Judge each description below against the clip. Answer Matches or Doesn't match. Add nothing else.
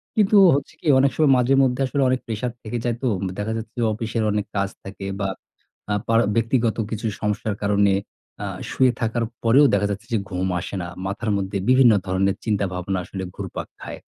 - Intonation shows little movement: Doesn't match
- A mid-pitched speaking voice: Doesn't match